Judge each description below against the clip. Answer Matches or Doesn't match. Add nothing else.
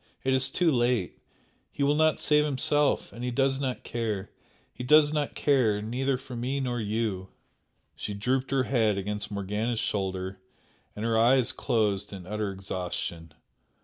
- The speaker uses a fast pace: Doesn't match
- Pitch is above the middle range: Doesn't match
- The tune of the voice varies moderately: Matches